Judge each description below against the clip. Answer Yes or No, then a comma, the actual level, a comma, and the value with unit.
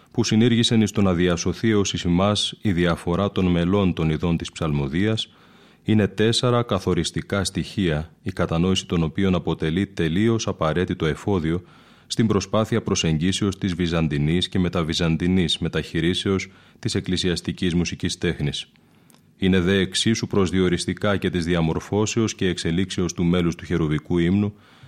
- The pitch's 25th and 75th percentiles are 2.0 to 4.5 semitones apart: Yes, average, 3.0 semitones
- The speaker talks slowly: No, average, 130 wpm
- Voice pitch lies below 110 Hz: Yes, very low, 90 Hz